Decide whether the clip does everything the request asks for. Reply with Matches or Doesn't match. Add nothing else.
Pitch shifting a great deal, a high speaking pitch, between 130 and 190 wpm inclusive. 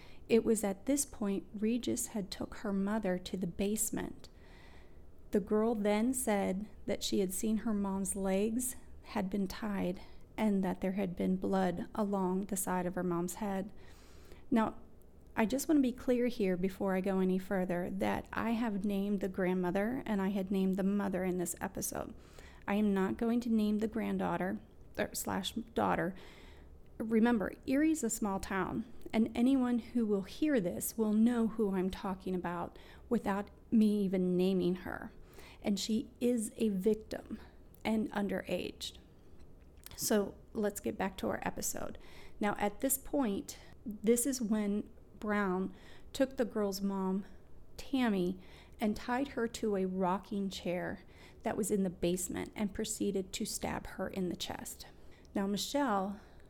Doesn't match